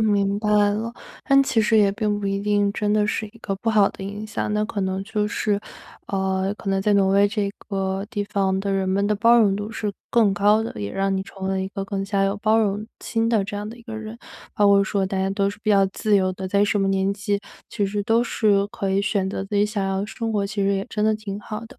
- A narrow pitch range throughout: Yes, narrow, 1.5 semitones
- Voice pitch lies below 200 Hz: No, high, 205 Hz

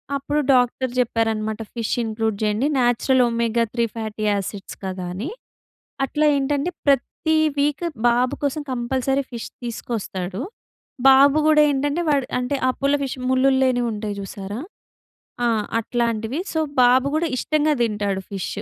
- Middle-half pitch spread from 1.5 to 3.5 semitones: No, average, 4.1 semitones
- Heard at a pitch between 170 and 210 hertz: No, high, 245 Hz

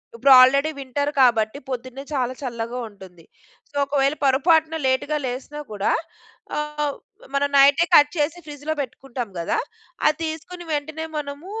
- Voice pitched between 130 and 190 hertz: No, very high, 280 Hz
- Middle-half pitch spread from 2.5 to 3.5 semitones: Yes, average, 2.8 semitones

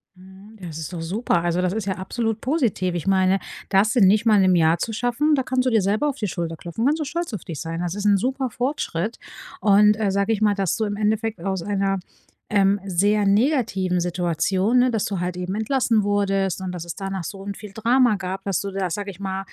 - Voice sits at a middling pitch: No, high, 200 Hz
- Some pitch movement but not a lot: Yes, average, 3.1 semitones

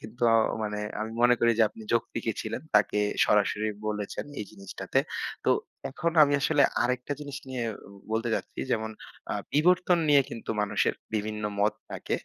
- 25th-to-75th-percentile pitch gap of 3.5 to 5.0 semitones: Yes, average, 4.7 semitones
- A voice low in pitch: Yes, low, 115 Hz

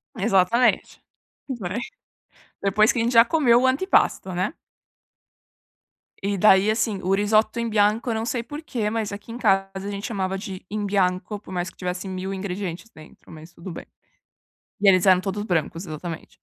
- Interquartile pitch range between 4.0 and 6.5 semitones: No, average, 3.4 semitones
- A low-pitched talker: No, high, 200 Hz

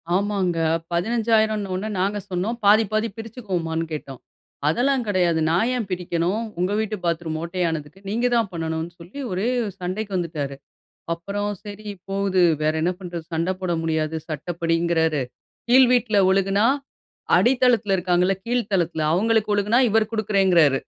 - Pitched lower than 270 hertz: Yes, high, 190 Hz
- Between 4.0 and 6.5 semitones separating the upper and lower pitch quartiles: Yes, average, 4.3 semitones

